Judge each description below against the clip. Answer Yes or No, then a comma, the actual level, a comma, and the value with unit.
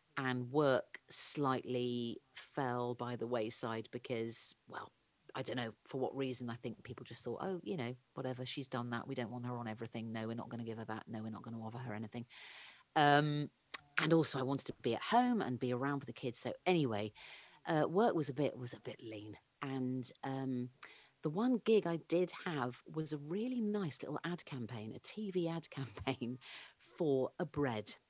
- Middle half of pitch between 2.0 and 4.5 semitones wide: Yes, average, 3.8 semitones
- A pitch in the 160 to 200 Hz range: No, low, 125 Hz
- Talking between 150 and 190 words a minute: No, fast, 205 wpm